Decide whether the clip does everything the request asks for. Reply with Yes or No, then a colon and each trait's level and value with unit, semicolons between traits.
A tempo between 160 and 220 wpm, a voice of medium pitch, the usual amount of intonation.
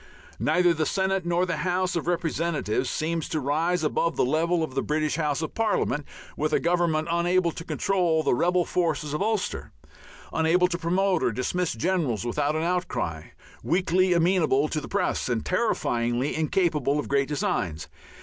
Yes: average, 170 wpm; medium, 165 Hz; average, 3.4 semitones